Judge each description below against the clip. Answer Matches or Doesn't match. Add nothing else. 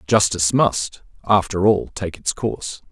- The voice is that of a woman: Doesn't match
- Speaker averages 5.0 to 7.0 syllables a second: Doesn't match